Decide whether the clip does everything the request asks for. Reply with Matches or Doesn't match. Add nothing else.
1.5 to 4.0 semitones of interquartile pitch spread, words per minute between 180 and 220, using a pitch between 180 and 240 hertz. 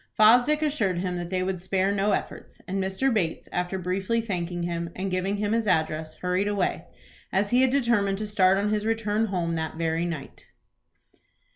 Matches